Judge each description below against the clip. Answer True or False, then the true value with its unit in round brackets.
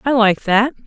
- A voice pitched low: False (230 Hz)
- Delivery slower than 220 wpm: True (210 wpm)